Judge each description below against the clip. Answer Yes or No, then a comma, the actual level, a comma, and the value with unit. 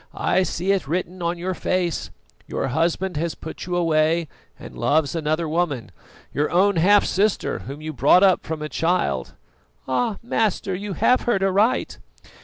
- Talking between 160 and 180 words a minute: Yes, average, 165 wpm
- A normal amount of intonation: Yes, average, 3.5 semitones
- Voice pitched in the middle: Yes, medium, 175 Hz